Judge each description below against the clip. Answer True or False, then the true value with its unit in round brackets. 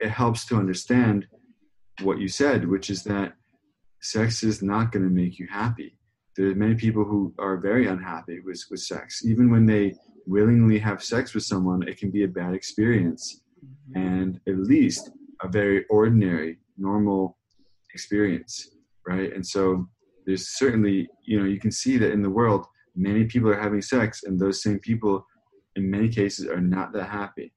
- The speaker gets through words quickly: False (175 wpm)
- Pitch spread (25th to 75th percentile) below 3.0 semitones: True (2.5 semitones)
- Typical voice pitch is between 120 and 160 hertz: False (100 Hz)